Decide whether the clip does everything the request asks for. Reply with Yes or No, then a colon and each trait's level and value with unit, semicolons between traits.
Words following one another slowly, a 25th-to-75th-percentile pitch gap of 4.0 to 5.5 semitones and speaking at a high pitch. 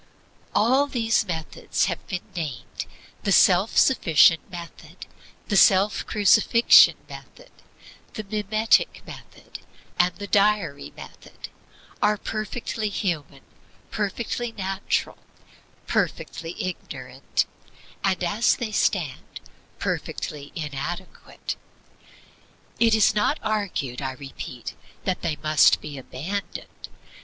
Yes: slow, 100 wpm; average, 5.0 semitones; high, 195 Hz